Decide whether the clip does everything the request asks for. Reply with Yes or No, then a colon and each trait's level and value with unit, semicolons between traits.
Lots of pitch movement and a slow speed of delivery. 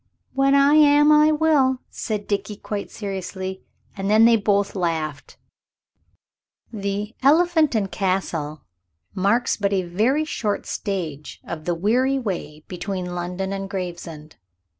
Yes: wide, 6.0 semitones; slow, 130 wpm